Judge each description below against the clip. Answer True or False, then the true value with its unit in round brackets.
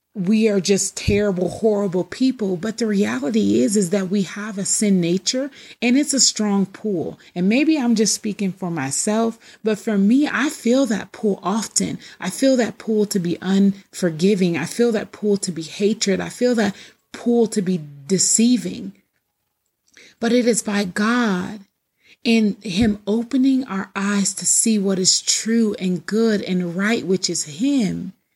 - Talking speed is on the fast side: False (170 wpm)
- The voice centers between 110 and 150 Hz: False (210 Hz)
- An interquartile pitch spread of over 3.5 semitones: False (3.1 semitones)